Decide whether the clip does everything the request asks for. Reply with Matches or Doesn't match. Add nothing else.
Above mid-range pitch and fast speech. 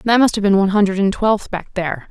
Matches